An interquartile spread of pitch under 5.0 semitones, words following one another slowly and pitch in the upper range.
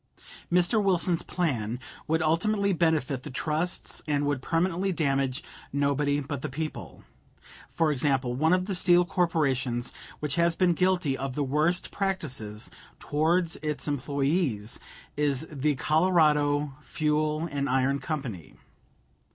No: average, 3.8 semitones; slow, 125 wpm; medium, 150 Hz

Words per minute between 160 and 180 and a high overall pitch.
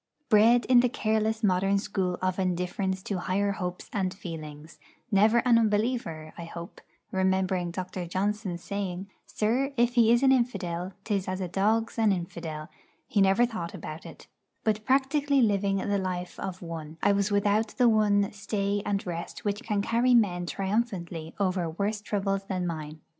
Yes: average, 165 wpm; high, 200 Hz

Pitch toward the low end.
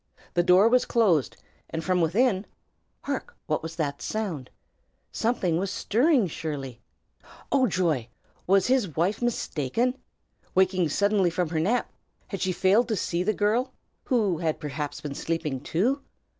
No: medium, 185 Hz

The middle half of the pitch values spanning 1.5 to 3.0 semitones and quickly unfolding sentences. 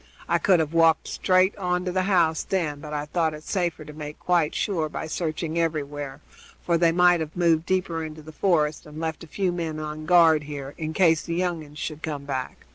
Yes: narrow, 2.5 semitones; fast, 220 wpm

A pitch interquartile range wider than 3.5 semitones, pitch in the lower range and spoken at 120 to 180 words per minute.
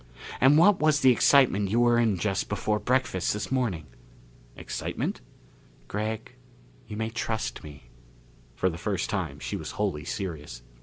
Yes: average, 5.2 semitones; low, 105 Hz; average, 150 wpm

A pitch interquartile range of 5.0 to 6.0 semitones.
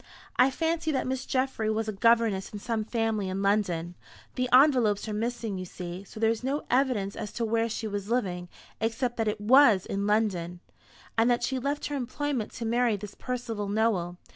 No: average, 3.6 semitones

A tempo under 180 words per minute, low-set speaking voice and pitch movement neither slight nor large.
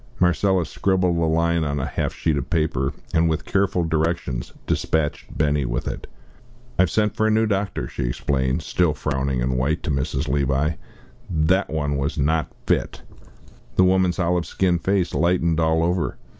Yes: average, 170 wpm; very low, 80 Hz; average, 3.7 semitones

